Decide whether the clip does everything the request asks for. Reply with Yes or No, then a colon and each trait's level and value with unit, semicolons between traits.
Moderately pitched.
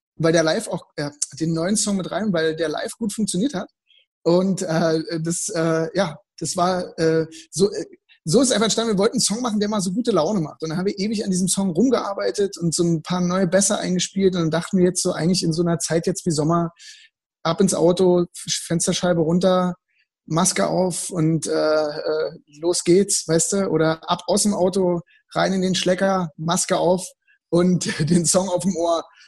Yes: medium, 180 Hz